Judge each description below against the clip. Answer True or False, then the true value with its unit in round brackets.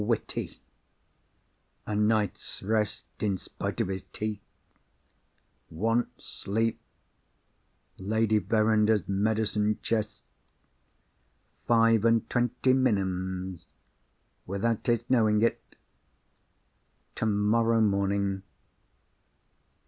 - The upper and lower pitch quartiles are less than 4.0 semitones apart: True (2.4 semitones)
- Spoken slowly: True (75 wpm)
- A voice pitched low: True (105 Hz)